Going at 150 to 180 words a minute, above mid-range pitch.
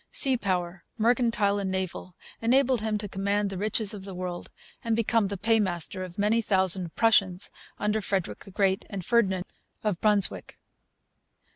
Yes: average, 155 wpm; high, 200 Hz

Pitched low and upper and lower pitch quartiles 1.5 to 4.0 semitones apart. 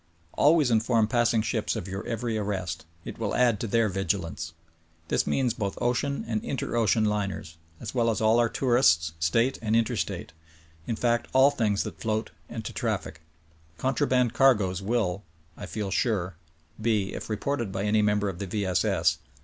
Yes: low, 110 Hz; average, 3.6 semitones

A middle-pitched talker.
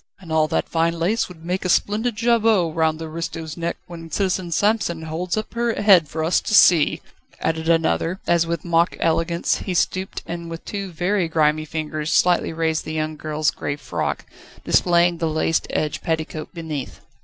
Yes: medium, 165 Hz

